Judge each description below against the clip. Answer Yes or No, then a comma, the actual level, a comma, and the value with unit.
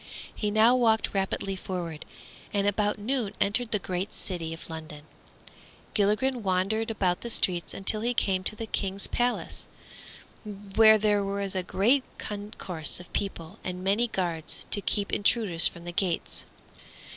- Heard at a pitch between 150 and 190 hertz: No, high, 200 Hz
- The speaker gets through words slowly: No, average, 150 wpm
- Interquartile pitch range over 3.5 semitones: No, average, 3.0 semitones